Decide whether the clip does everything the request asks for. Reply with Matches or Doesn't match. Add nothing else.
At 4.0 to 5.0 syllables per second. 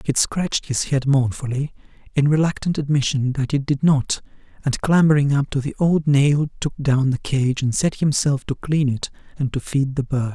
Matches